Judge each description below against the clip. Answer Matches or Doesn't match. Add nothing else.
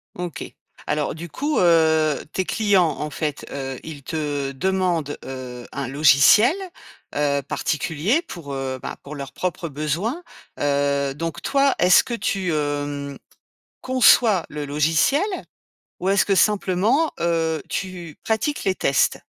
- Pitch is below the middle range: Doesn't match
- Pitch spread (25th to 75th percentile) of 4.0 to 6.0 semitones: Matches